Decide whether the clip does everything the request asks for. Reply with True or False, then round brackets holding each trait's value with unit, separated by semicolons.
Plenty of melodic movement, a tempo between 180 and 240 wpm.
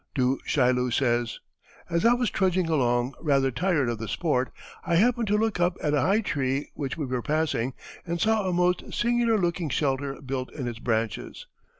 True (6.1 semitones; 190 wpm)